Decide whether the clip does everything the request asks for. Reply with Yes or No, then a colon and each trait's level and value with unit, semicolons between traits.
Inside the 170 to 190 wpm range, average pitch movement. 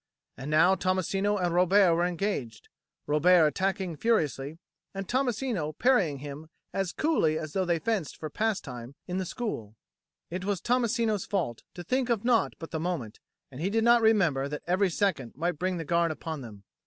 Yes: average, 180 wpm; average, 5.0 semitones